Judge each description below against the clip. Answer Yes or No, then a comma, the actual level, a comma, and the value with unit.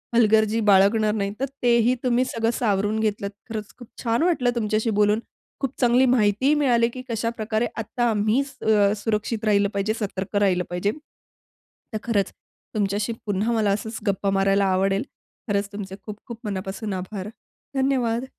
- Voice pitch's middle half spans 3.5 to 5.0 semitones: No, average, 2.7 semitones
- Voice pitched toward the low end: No, high, 215 Hz